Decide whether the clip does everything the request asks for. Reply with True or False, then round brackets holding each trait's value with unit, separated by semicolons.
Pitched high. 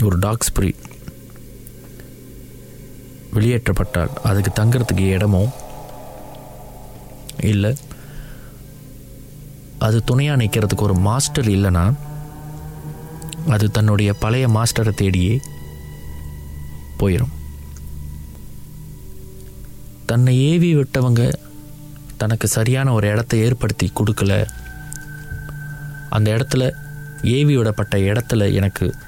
False (115 Hz)